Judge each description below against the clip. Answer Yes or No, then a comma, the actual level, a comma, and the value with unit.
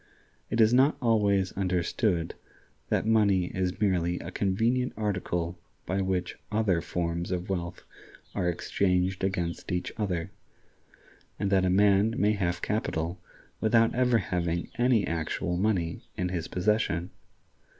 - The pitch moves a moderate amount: Yes, average, 3.3 semitones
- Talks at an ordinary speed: No, slow, 130 wpm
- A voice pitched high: No, very low, 95 Hz